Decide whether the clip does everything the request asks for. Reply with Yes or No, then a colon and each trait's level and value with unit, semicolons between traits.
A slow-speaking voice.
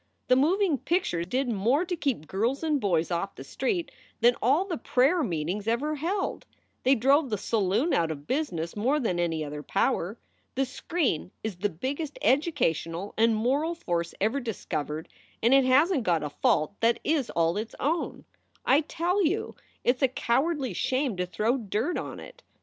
No: average, 180 wpm